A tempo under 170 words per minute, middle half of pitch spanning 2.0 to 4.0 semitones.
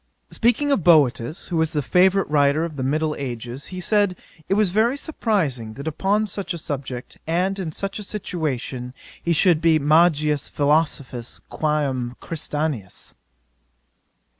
No: average, 150 wpm; average, 5.0 semitones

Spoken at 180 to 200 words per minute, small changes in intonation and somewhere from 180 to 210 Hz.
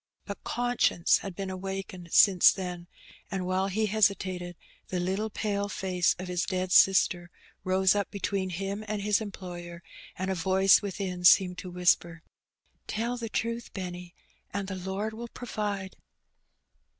No: average, 150 wpm; narrow, 2.1 semitones; high, 190 Hz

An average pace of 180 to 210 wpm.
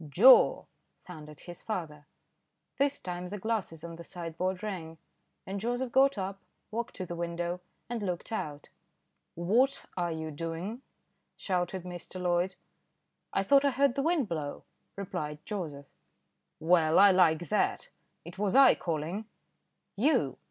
No: average, 140 wpm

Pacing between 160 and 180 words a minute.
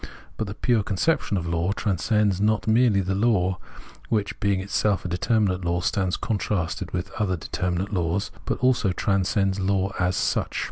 Yes: average, 170 wpm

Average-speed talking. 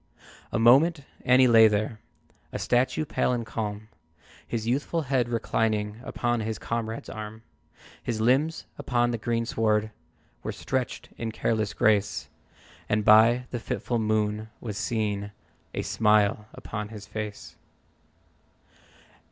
No: slow, 125 wpm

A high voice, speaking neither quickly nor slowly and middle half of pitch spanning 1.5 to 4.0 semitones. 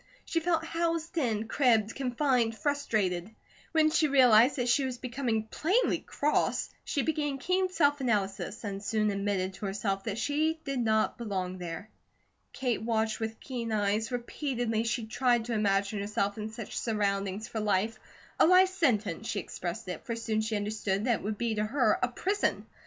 No: high, 225 Hz; average, 175 wpm; average, 4.6 semitones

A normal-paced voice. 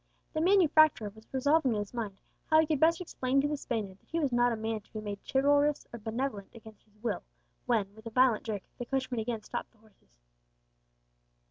No: fast, 215 wpm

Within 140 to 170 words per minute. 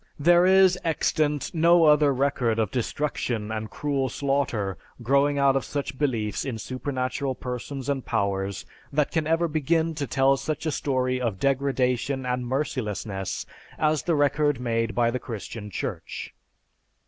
Yes: average, 150 wpm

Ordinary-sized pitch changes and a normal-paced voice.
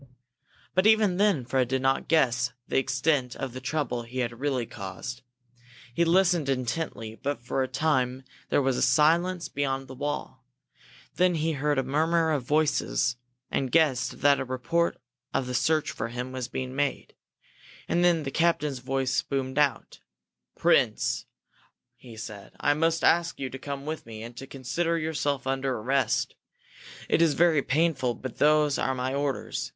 Yes: average, 3.6 semitones; average, 165 wpm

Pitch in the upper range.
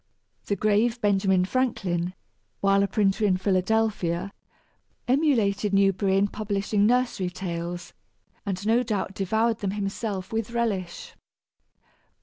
Yes: high, 200 Hz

